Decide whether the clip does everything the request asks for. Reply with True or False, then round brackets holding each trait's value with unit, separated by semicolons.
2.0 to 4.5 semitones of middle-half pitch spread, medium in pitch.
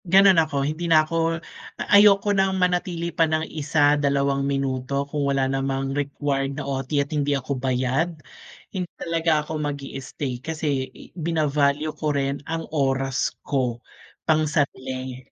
True (3.0 semitones; 145 Hz)